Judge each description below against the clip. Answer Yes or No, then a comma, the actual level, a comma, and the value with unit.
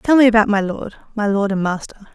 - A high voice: Yes, high, 210 Hz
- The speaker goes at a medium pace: No, fast, 225 wpm